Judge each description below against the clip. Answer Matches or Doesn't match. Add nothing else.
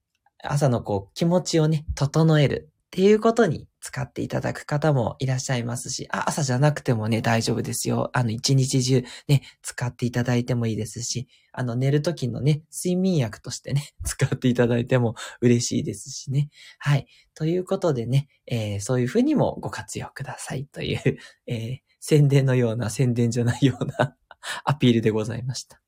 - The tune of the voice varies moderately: Matches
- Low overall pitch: Matches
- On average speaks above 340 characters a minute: Matches